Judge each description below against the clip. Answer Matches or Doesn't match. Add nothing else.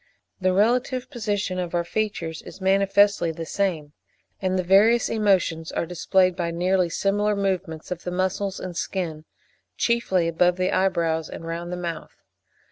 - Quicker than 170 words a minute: Doesn't match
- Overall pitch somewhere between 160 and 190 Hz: Matches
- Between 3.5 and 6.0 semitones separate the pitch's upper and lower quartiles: Doesn't match